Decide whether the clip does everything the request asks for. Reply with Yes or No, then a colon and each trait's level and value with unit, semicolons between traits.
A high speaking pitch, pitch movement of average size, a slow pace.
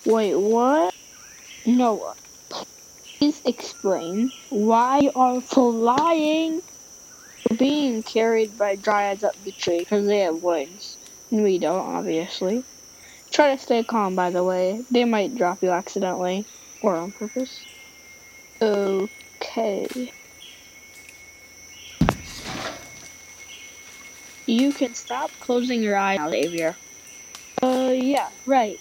Yes: high, 225 Hz; average, 4.7 semitones; slow, 110 wpm